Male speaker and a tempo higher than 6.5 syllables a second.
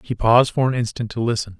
Yes: male; 6.7 syllables/s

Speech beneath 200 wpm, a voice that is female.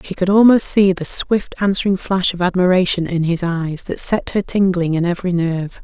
No: fast, 205 wpm; female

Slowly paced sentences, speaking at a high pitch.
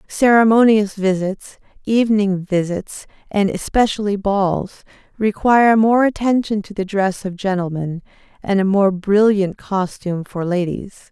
Yes: slow, 120 wpm; high, 200 Hz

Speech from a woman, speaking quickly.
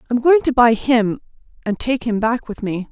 Yes: female; fast, 225 wpm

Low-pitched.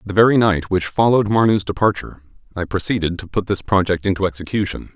Yes: low, 100 Hz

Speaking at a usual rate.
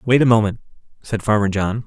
Yes: average, 195 wpm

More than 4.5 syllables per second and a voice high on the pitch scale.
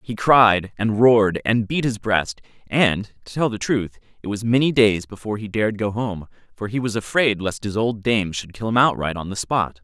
No: 4.9 syllables/s; low, 105 Hz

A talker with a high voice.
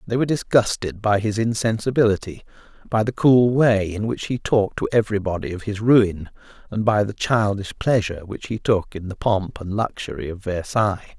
No: low, 105 Hz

